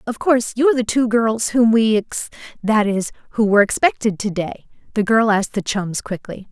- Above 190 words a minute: Yes, fast, 205 wpm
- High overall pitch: Yes, high, 215 Hz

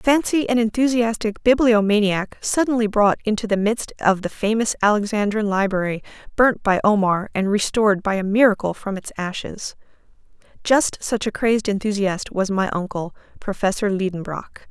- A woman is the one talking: Yes, female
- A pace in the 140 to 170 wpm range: Yes, average, 145 wpm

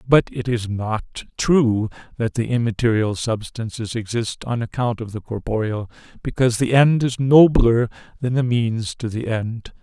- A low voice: Yes, low, 115 Hz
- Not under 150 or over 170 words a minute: Yes, average, 160 wpm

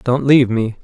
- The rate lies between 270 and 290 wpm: No, fast, 215 wpm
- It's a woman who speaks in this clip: No, male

